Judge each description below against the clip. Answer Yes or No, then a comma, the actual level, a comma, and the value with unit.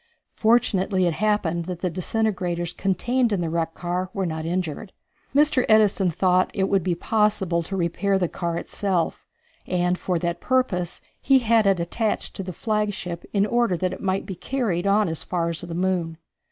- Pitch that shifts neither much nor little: Yes, average, 3.5 semitones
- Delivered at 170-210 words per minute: Yes, average, 185 wpm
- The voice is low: No, medium, 185 Hz